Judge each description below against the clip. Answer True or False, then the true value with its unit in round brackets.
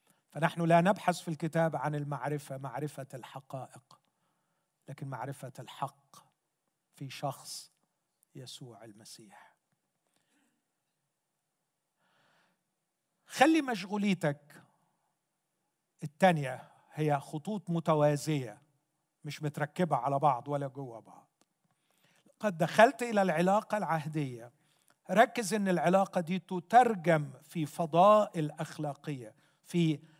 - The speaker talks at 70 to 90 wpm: True (85 wpm)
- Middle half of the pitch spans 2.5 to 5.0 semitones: True (4.1 semitones)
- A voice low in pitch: False (160 Hz)